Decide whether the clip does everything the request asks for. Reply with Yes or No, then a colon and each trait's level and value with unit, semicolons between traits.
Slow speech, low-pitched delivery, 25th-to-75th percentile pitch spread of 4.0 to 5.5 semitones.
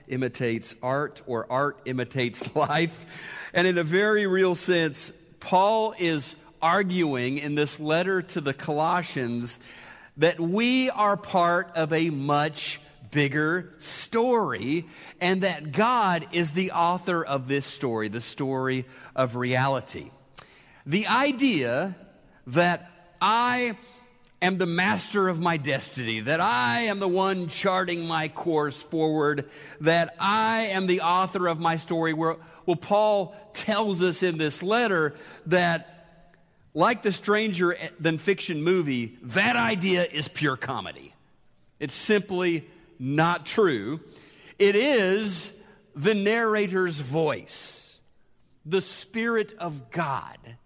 No: slow, 120 wpm; medium, 170 Hz; average, 4.3 semitones